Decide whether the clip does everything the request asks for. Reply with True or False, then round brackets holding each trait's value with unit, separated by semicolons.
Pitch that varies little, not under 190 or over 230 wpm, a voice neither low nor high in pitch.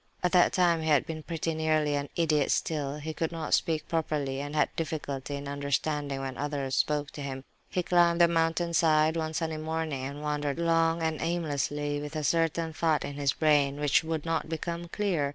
True (2.2 semitones; 200 wpm; 155 Hz)